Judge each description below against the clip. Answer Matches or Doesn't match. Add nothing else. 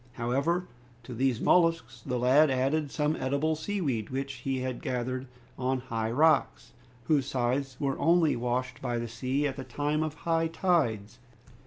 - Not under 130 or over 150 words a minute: Doesn't match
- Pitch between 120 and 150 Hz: Matches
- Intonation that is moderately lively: Matches